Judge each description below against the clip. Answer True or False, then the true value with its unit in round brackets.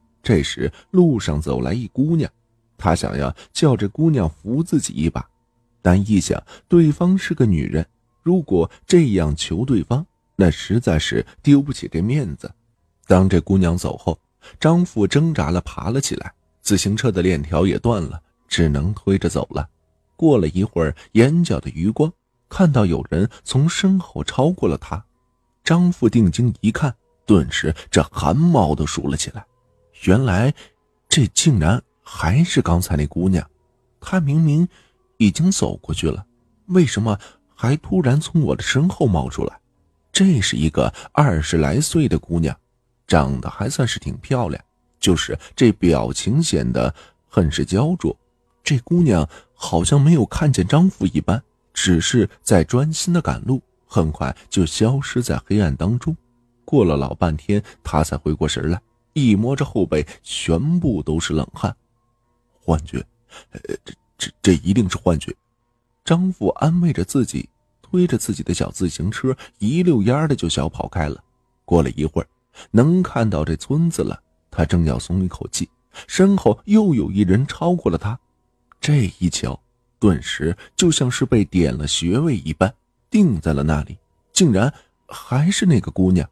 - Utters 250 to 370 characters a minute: False (225 characters per minute)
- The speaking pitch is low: True (110 Hz)